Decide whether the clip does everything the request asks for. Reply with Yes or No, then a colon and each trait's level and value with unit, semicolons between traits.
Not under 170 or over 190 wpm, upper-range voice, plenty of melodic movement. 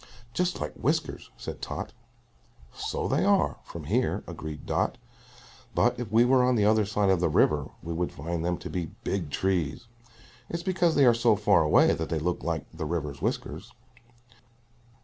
No: average, 180 wpm; very low, 90 Hz; wide, 6.5 semitones